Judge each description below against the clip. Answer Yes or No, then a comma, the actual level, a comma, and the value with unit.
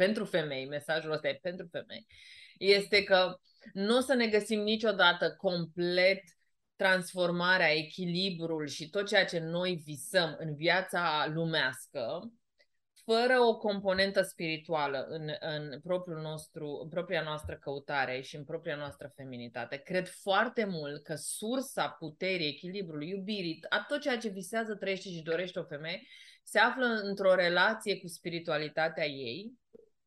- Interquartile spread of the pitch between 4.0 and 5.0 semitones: Yes, average, 4.3 semitones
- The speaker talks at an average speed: Yes, average, 140 wpm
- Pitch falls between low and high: Yes, medium, 180 Hz